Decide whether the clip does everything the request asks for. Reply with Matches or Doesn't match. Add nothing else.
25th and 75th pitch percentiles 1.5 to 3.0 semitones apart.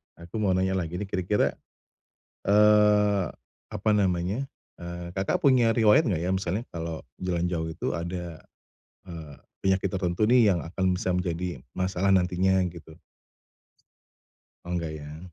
Matches